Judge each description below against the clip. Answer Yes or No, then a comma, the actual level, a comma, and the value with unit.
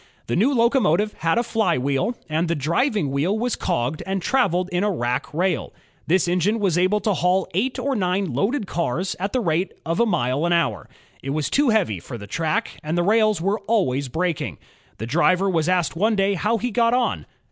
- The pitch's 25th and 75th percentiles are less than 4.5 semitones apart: No, average, 5.1 semitones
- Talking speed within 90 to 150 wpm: No, fast, 205 wpm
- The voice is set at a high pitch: No, medium, 180 Hz